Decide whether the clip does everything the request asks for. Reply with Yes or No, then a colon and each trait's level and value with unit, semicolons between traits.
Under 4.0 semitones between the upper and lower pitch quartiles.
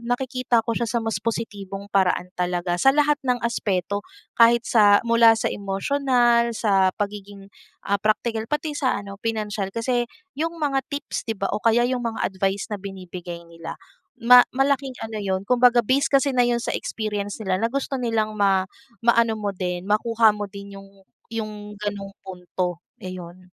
Yes: average, 3.5 semitones